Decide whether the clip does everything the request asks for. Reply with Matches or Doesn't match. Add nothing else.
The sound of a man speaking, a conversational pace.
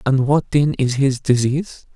Matches